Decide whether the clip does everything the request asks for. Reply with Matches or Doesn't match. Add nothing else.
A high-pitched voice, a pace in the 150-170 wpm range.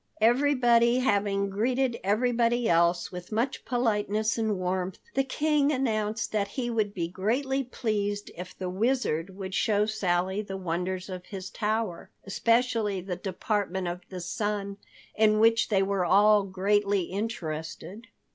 Doesn't match